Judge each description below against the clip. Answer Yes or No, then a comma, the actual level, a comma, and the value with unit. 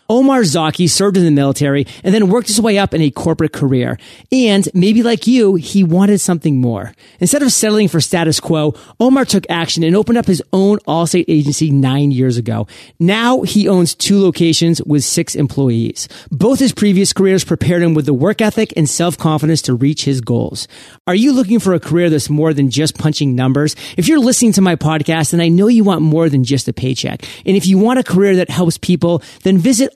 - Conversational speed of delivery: No, fast, 215 wpm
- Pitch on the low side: No, medium, 170 Hz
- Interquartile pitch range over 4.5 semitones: Yes, average, 5.2 semitones